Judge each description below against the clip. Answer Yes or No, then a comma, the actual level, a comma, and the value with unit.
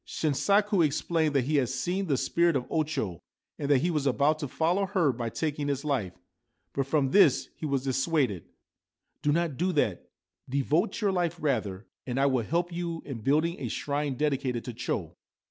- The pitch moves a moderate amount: Yes, average, 4.1 semitones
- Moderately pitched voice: Yes, medium, 145 Hz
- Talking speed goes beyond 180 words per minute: Yes, average, 195 wpm